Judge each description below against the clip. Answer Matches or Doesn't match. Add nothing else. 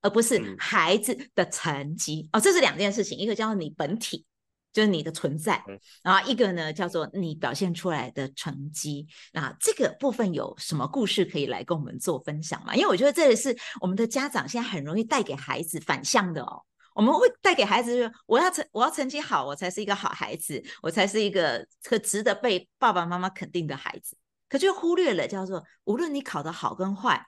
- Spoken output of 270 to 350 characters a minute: Matches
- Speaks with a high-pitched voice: Matches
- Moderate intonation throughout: Doesn't match